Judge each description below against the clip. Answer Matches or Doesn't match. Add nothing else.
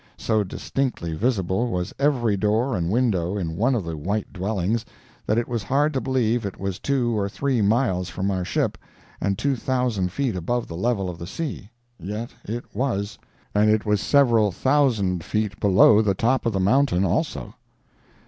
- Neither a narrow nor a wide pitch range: Matches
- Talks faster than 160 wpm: Matches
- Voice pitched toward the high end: Doesn't match